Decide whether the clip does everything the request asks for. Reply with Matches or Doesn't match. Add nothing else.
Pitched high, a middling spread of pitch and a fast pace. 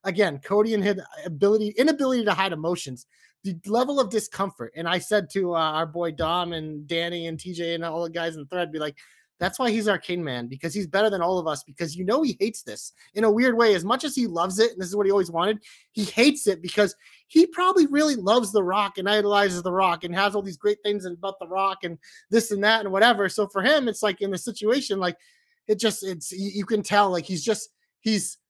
Matches